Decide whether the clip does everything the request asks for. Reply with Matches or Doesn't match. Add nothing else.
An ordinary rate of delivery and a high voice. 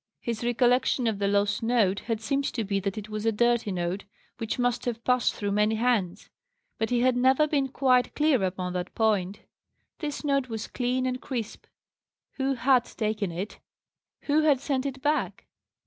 Matches